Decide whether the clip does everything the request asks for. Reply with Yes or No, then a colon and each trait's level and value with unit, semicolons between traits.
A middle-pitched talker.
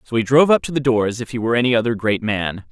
No: low, 115 Hz